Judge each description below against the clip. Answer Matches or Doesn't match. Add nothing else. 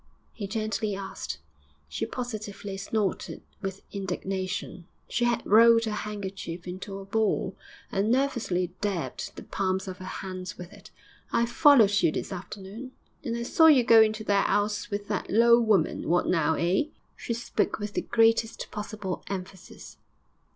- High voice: Matches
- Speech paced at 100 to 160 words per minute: Matches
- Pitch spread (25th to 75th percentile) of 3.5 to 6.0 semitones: Doesn't match